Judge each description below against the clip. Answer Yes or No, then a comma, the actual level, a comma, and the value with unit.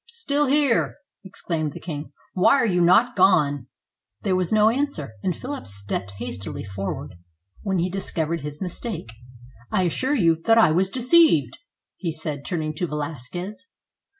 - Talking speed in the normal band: Yes, average, 165 wpm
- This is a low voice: No, medium, 180 Hz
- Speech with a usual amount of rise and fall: No, wide, 7.0 semitones